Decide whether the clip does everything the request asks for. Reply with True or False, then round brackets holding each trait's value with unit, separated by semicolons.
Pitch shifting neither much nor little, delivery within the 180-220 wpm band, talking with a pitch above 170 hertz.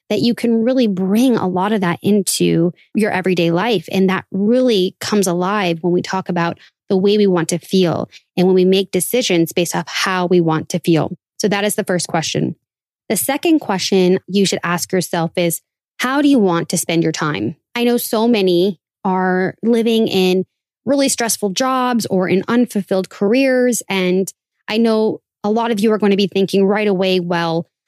True (3.6 semitones; 195 wpm; 190 Hz)